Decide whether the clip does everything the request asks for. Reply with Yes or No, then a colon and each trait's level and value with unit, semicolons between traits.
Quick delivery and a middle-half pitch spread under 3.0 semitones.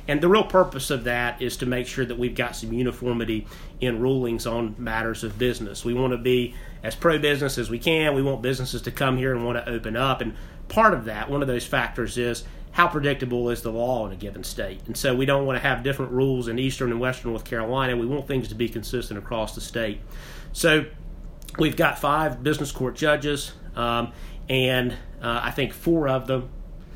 Yes: fast, 220 wpm; narrow, 2.4 semitones